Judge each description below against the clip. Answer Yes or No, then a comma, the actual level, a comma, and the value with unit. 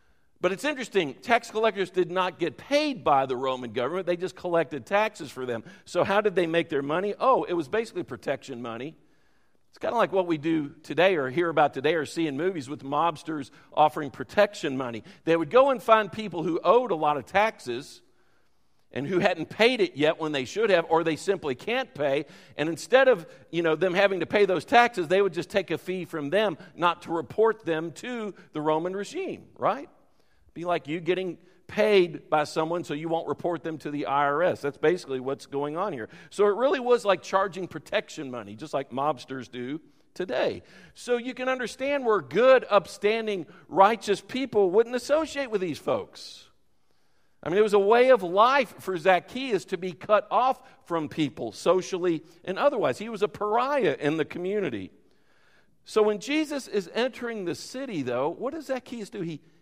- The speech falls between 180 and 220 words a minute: Yes, average, 195 wpm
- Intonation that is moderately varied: No, wide, 5.8 semitones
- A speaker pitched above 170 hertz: Yes, medium, 185 Hz